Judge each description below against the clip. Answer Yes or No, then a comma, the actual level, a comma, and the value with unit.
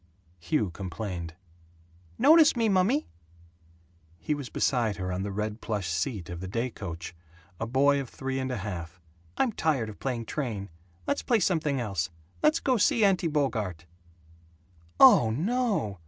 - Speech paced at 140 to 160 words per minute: Yes, average, 155 wpm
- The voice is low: Yes, low, 115 Hz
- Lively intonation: Yes, wide, 8.8 semitones